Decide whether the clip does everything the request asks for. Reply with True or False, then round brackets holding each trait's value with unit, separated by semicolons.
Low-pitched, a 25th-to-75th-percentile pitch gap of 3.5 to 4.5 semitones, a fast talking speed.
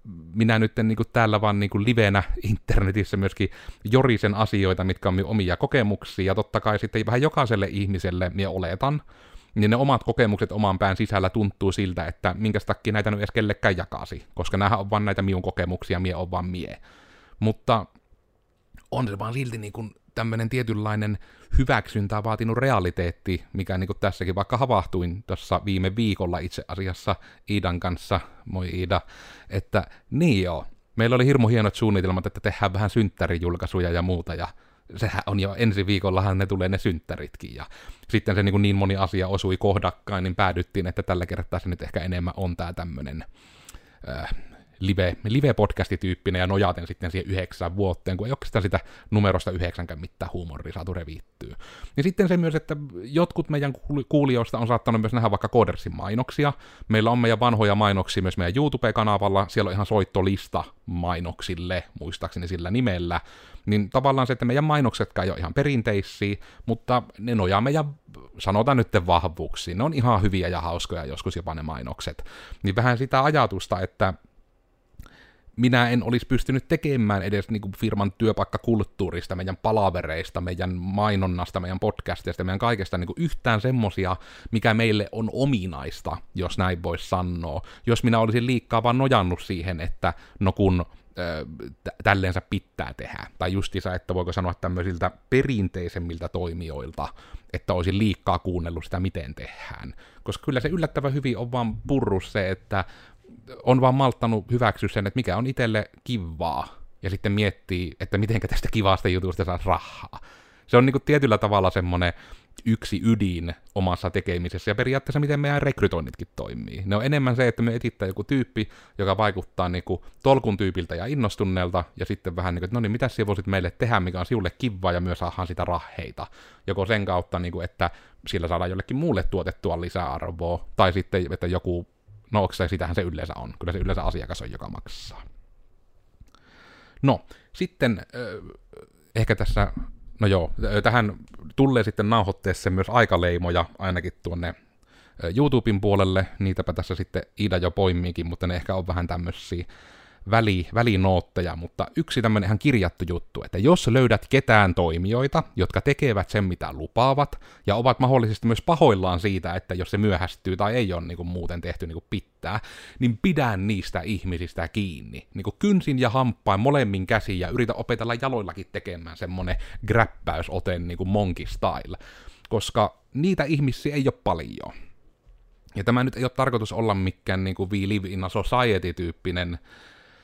True (100 Hz; 4.0 semitones; 165 wpm)